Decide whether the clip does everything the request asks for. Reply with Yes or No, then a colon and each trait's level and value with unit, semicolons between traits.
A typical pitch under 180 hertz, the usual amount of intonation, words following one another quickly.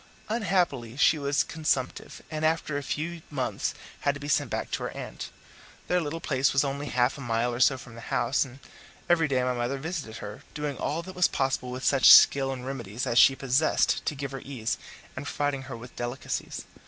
Yes: low, 135 Hz; average, 3.1 semitones; fast, 210 wpm